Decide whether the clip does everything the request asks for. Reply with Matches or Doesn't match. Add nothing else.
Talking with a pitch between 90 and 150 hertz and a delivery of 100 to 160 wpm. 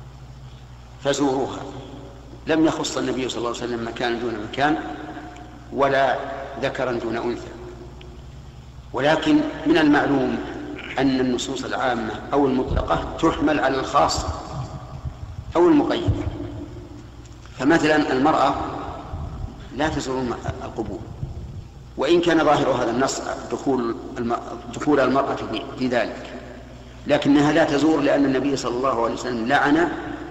Matches